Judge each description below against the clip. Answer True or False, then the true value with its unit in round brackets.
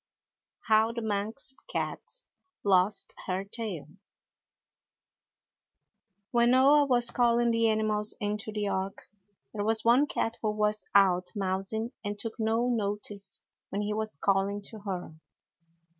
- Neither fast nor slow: False (130 wpm)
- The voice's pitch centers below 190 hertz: False (215 Hz)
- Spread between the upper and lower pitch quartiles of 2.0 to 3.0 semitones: True (2.4 semitones)